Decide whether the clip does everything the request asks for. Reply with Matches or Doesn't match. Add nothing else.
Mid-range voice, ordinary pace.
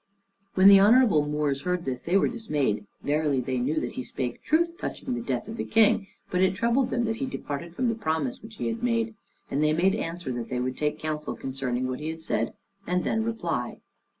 Doesn't match